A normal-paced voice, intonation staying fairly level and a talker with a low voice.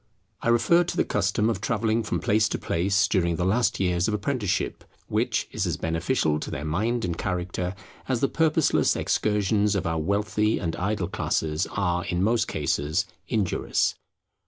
No: average, 170 wpm; average, 4.0 semitones; low, 100 Hz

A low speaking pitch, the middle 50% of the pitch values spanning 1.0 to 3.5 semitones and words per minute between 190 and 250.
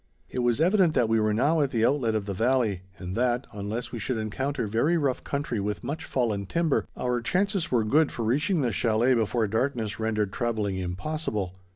No: low, 120 Hz; average, 4.7 semitones; average, 200 wpm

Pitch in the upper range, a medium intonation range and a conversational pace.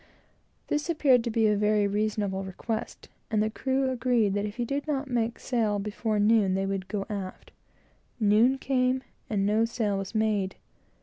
Yes: high, 215 Hz; average, 3.2 semitones; average, 175 wpm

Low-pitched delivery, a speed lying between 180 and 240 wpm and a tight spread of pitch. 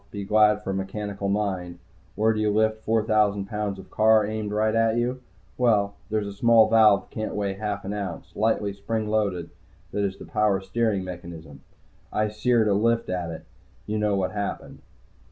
Yes: low, 105 Hz; average, 195 wpm; narrow, 1.7 semitones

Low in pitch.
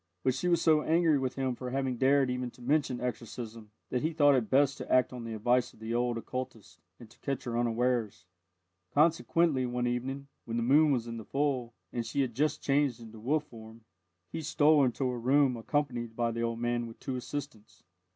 Yes: low, 125 Hz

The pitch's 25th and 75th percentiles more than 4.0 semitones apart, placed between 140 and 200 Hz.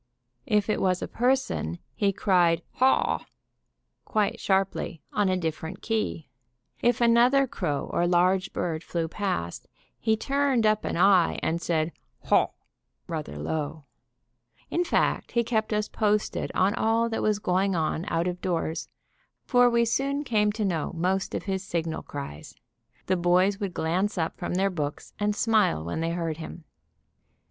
Yes: average, 4.6 semitones; high, 190 Hz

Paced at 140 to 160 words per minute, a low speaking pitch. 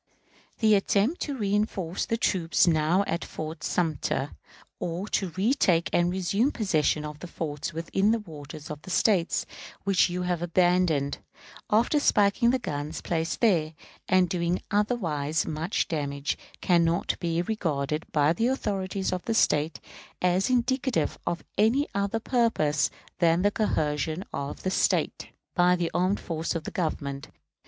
No: average, 150 wpm; medium, 175 Hz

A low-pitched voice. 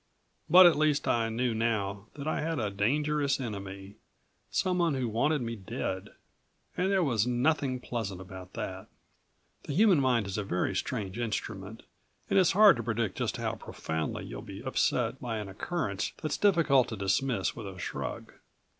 Yes: low, 115 Hz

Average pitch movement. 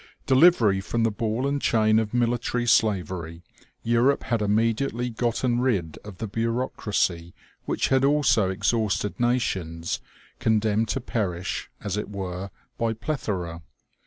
Yes: average, 3.7 semitones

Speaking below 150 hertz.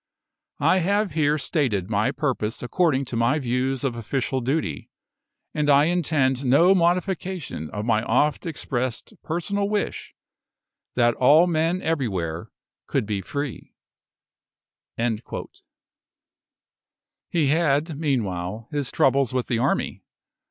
Yes: low, 135 Hz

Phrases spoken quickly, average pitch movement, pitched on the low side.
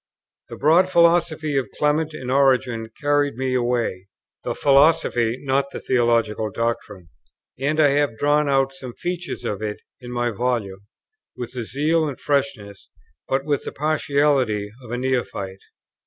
No: average, 150 wpm; average, 3.9 semitones; low, 130 Hz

